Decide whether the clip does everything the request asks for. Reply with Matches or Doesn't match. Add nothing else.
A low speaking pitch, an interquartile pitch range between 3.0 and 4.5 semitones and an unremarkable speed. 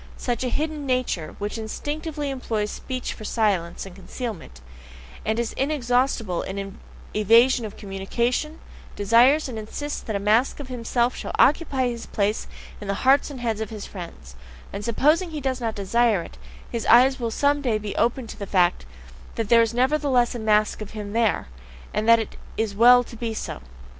Doesn't match